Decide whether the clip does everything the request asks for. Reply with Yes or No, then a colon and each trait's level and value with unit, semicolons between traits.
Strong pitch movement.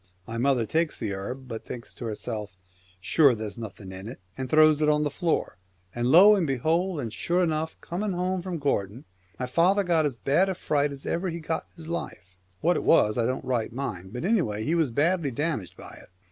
Yes: wide, 6.6 semitones